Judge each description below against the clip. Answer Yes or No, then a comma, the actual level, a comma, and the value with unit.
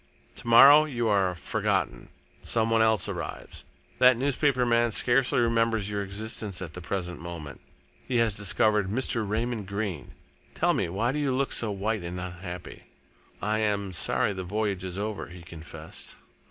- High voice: No, low, 105 Hz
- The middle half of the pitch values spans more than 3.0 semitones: Yes, average, 4.1 semitones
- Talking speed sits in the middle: Yes, average, 165 wpm